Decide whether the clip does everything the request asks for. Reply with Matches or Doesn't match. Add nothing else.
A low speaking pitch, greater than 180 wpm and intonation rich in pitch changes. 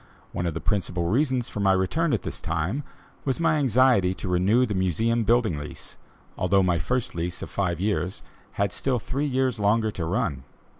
Matches